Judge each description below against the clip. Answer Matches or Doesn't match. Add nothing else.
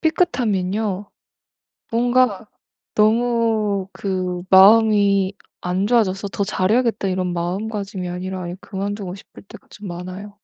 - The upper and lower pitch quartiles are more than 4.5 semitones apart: Doesn't match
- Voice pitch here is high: Matches